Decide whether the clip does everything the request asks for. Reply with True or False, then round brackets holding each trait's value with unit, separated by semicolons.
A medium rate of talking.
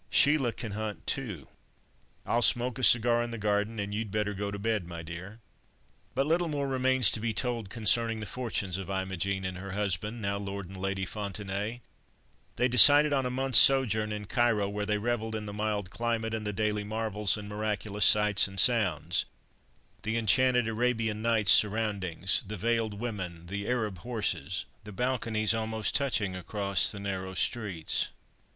True (170 wpm)